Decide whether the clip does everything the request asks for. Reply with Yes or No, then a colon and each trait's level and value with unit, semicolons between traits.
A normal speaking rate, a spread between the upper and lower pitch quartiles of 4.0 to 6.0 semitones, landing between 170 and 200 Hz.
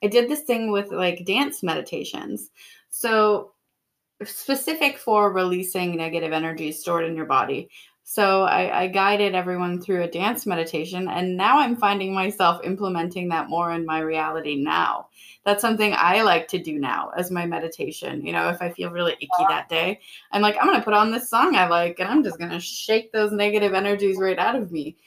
No: average, 195 wpm; average, 3.6 semitones; medium, 185 Hz